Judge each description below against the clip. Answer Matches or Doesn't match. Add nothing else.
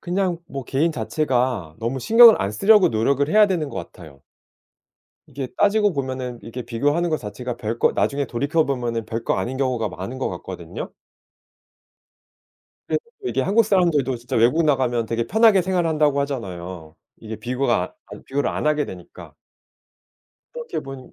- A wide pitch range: Matches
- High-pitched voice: Doesn't match